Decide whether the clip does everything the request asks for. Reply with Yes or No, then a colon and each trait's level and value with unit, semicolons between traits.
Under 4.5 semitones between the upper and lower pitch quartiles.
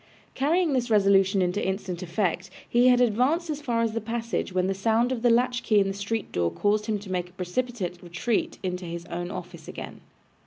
No: average, 4.8 semitones